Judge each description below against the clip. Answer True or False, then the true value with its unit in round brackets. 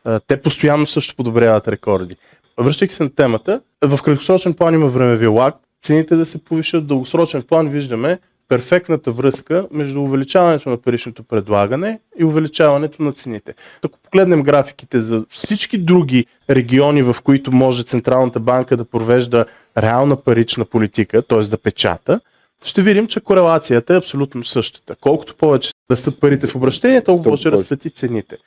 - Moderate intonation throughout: True (4.9 semitones)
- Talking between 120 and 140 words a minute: False (155 wpm)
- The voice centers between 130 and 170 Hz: True (140 Hz)